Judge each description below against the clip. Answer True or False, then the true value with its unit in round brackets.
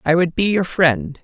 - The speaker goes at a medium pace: False (245 wpm)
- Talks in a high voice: False (160 Hz)